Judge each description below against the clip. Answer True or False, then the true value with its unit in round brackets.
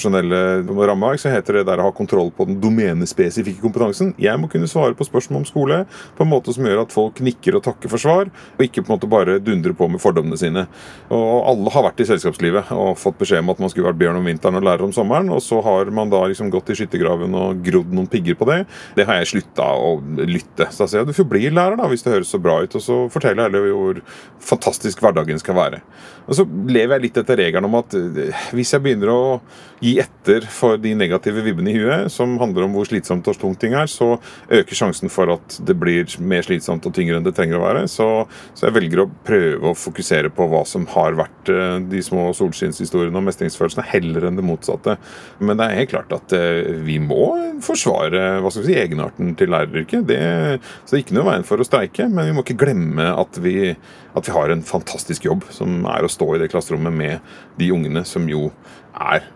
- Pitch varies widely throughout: True (6.7 semitones)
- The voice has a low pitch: True (105 Hz)